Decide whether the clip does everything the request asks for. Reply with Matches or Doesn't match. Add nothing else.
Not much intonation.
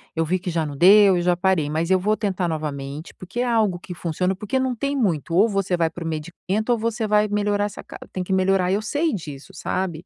Doesn't match